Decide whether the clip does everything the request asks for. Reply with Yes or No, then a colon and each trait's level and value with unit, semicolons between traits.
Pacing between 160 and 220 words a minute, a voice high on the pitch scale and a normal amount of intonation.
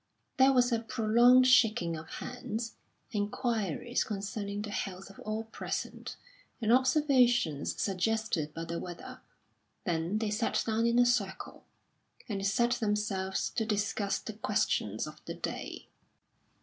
No: slow, 135 wpm; high, 215 Hz; average, 3.5 semitones